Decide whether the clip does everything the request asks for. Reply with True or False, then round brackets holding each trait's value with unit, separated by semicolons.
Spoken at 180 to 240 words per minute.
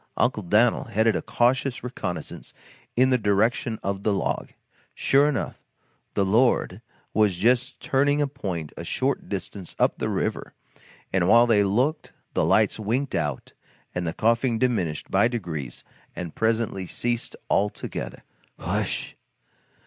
False (140 wpm)